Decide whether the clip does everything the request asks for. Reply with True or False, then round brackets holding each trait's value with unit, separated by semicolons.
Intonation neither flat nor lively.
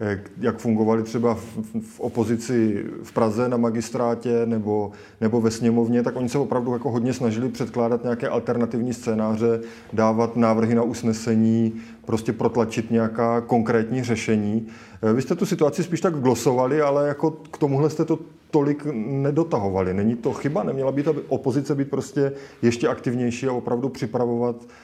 True (3.1 semitones)